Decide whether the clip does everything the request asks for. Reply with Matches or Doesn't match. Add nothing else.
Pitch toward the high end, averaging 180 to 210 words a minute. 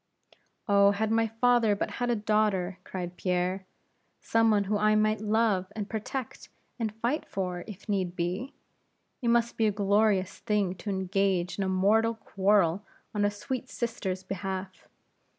Doesn't match